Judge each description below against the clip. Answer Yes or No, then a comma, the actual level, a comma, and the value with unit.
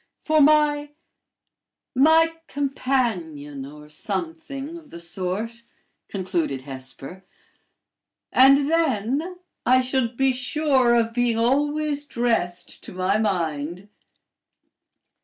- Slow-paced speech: Yes, slow, 100 wpm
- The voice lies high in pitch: Yes, high, 240 Hz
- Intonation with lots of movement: Yes, wide, 8.0 semitones